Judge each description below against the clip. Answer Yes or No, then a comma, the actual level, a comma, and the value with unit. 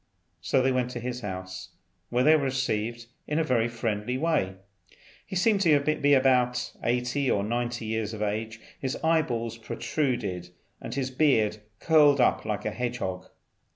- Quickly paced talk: No, average, 170 wpm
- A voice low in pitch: Yes, low, 125 Hz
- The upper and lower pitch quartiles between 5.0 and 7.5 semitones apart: No, average, 4.0 semitones